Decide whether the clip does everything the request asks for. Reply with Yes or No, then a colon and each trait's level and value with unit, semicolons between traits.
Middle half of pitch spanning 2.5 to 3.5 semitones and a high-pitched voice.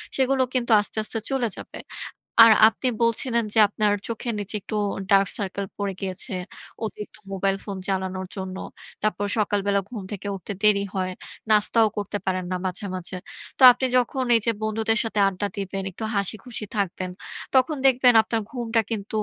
Yes: average, 2.9 semitones; high, 210 Hz